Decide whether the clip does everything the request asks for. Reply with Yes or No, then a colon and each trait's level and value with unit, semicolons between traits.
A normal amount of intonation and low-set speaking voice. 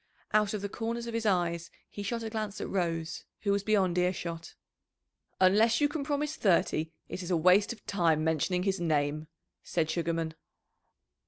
No: average, 4.3 semitones; medium, 185 Hz